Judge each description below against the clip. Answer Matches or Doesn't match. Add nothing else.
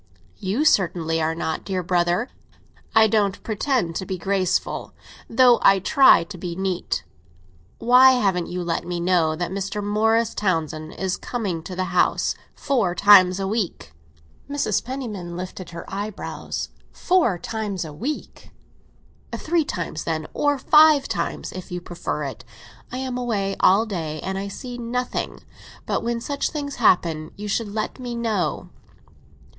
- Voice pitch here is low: Doesn't match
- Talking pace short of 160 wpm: Matches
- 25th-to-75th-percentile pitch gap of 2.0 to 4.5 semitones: Doesn't match